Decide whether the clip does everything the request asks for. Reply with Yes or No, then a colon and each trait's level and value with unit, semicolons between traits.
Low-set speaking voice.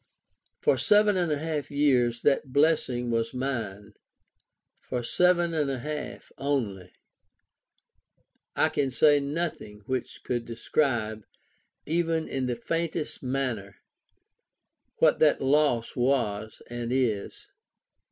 Yes: low, 130 Hz